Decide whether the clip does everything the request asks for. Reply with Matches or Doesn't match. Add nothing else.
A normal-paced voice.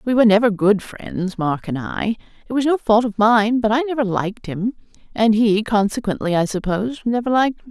Doesn't match